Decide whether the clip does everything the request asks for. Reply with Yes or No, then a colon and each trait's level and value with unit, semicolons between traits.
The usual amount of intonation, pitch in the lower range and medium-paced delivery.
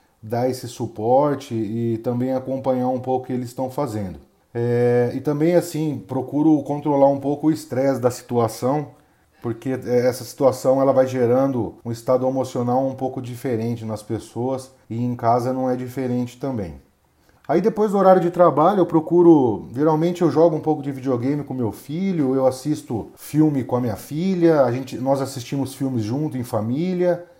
Yes: average, 3.4 semitones; low, 130 Hz; average, 175 wpm